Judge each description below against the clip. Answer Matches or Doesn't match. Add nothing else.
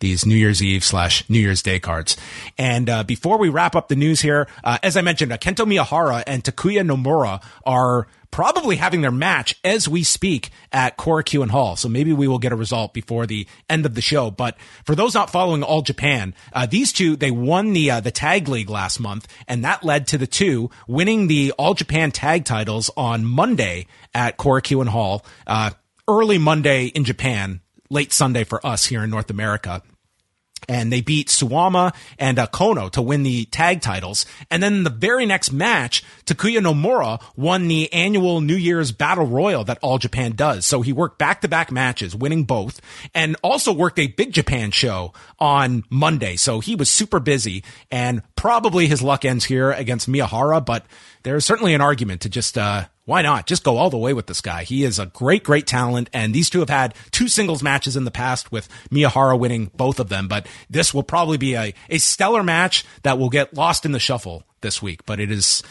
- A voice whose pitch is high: Doesn't match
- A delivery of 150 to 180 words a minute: Doesn't match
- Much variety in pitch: Matches